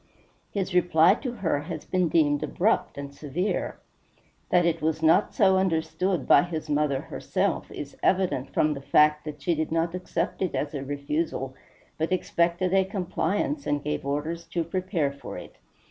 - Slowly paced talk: No, average, 170 wpm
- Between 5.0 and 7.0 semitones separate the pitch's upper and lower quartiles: No, average, 3.5 semitones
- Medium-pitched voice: Yes, medium, 165 Hz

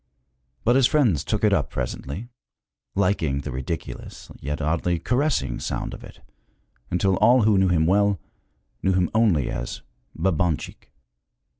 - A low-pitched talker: Yes, very low, 90 Hz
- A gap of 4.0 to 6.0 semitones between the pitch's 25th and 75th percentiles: Yes, wide, 5.5 semitones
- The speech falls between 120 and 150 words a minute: Yes, average, 140 wpm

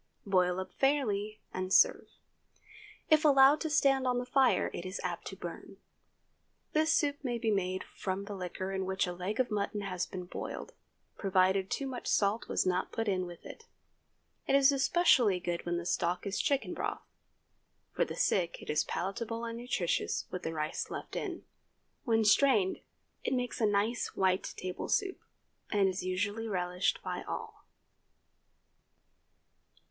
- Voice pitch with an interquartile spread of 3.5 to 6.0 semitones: Yes, average, 5.1 semitones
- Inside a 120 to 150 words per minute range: No, average, 165 wpm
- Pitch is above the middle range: Yes, high, 200 Hz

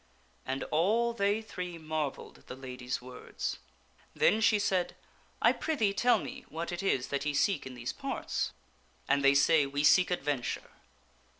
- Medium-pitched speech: Yes, medium, 155 Hz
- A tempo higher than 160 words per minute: Yes, average, 170 wpm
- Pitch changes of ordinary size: No, wide, 6.4 semitones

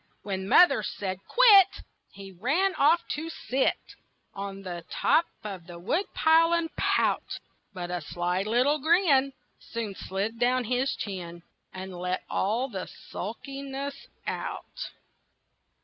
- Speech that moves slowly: Yes, slow, 125 wpm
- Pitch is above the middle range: Yes, high, 230 Hz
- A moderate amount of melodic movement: No, wide, 7.8 semitones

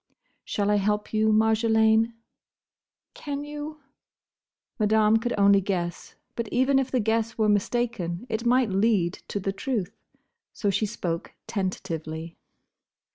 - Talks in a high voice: Yes, high, 215 Hz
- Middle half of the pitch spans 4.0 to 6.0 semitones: No, average, 3.0 semitones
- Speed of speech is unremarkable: No, slow, 130 wpm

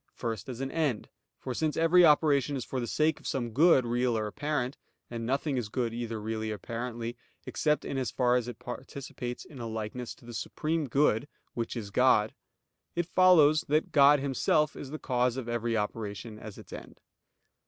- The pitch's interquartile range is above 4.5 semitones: No, average, 4.0 semitones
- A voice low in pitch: Yes, low, 125 Hz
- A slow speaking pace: No, average, 195 wpm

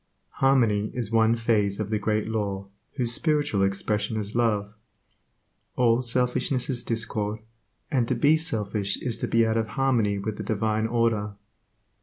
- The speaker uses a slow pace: No, average, 155 wpm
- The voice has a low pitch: Yes, low, 110 Hz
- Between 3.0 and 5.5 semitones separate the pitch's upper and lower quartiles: No, narrow, 2.5 semitones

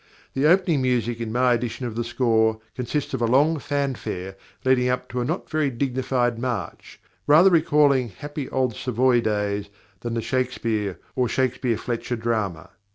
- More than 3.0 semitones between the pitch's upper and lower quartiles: No, narrow, 2.5 semitones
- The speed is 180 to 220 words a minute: No, average, 160 wpm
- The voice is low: Yes, low, 125 Hz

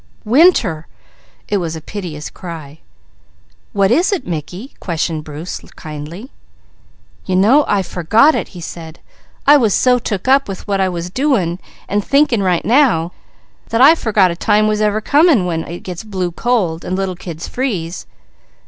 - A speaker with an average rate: Yes, average, 165 wpm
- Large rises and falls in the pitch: Yes, wide, 6.0 semitones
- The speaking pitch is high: Yes, high, 195 Hz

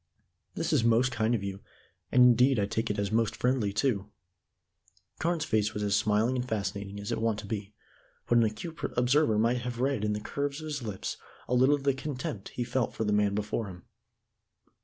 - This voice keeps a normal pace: No, fast, 215 wpm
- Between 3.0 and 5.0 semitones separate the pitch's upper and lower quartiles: Yes, average, 3.5 semitones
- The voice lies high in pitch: No, low, 115 Hz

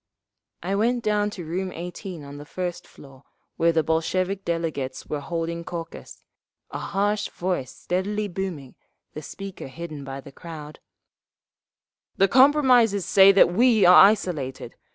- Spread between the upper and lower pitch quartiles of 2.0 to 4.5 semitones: Yes, average, 4.1 semitones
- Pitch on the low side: No, medium, 180 Hz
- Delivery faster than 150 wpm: No, average, 140 wpm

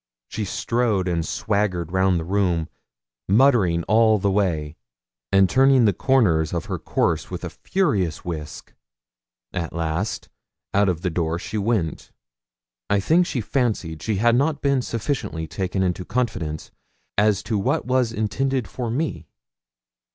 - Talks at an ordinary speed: Yes, average, 145 wpm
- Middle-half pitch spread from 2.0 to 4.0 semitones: No, wide, 5.6 semitones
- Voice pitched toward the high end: No, low, 100 Hz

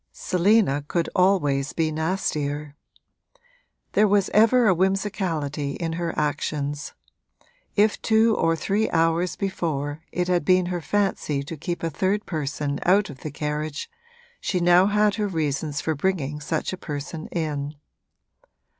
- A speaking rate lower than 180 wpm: Yes, average, 140 wpm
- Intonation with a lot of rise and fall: No, average, 4.4 semitones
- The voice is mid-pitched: Yes, medium, 165 Hz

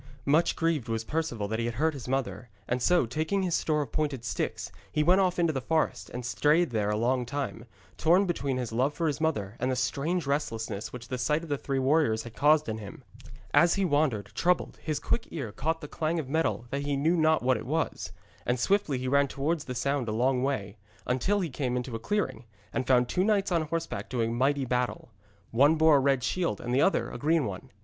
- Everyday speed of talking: No, fast, 230 wpm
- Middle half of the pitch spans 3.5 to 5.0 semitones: Yes, average, 4.6 semitones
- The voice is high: No, medium, 140 Hz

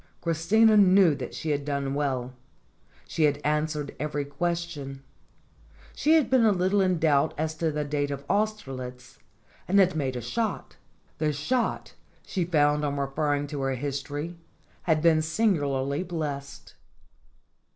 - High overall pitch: No, medium, 150 Hz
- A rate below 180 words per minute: Yes, average, 145 wpm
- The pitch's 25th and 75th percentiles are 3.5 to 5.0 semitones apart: Yes, average, 3.9 semitones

